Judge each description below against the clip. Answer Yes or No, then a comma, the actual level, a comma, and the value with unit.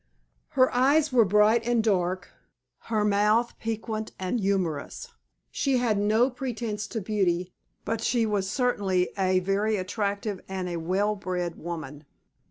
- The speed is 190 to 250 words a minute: No, average, 145 wpm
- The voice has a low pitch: No, high, 210 Hz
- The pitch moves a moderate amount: Yes, average, 3.6 semitones